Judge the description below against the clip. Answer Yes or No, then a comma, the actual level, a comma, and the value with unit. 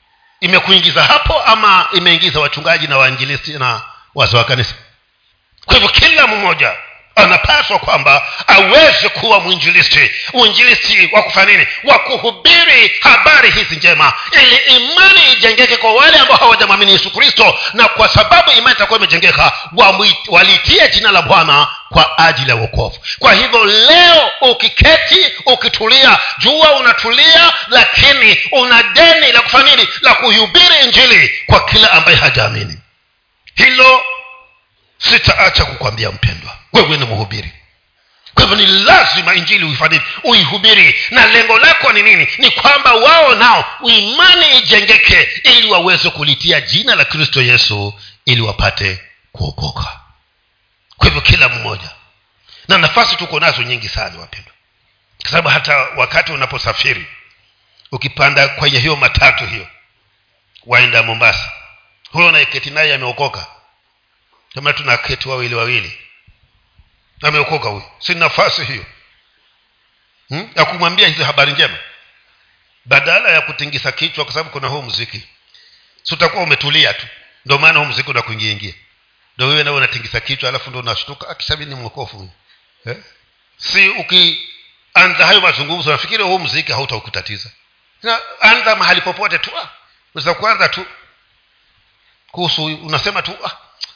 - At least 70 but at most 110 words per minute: Yes, average, 105 wpm